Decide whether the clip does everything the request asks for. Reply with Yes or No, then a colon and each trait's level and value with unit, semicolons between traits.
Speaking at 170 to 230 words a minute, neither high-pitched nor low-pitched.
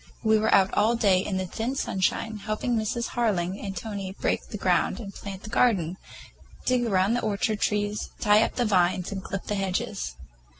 No: average, 185 wpm; high, 205 Hz